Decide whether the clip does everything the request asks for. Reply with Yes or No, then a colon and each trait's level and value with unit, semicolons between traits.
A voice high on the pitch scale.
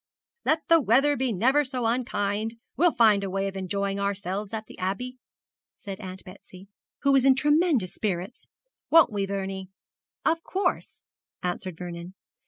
Yes: high, 205 Hz